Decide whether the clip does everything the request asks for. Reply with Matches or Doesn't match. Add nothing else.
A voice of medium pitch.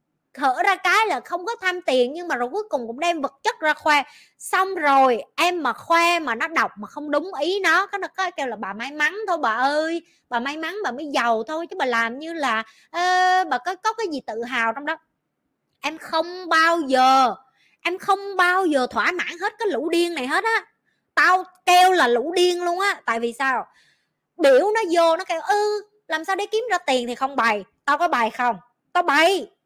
Doesn't match